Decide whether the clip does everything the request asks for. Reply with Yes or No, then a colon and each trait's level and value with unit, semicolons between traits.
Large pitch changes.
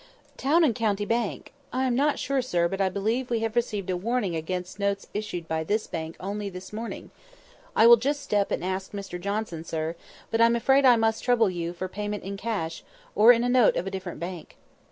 No: average, 4.3 semitones